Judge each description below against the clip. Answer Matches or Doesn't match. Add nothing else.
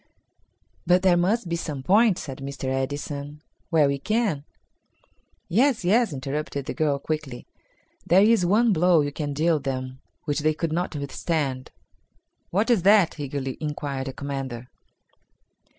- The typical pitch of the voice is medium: Matches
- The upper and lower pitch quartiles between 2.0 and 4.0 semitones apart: Doesn't match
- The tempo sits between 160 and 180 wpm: Doesn't match